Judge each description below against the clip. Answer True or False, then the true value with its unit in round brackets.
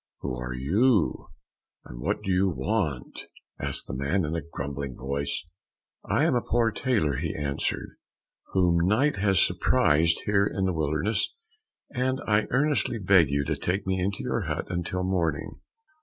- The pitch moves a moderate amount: False (6.0 semitones)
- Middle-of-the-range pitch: False (90 Hz)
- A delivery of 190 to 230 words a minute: False (160 wpm)